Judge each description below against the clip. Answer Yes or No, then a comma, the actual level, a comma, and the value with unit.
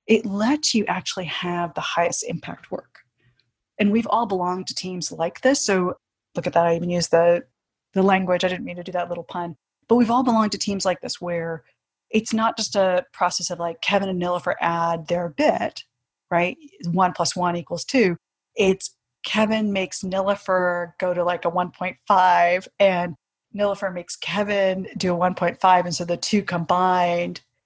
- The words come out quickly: No, average, 180 wpm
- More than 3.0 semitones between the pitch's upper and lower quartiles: No, average, 2.7 semitones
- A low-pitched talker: No, medium, 180 Hz